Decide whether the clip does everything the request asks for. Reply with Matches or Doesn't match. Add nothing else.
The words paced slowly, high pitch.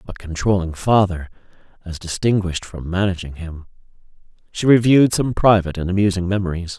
Doesn't match